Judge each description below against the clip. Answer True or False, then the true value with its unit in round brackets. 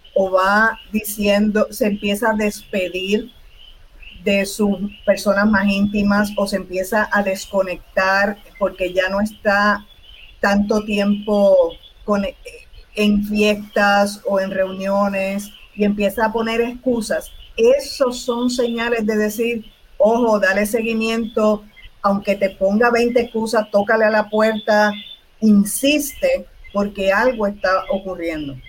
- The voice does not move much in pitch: True (2.1 semitones)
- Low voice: False (210 Hz)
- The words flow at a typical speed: False (115 wpm)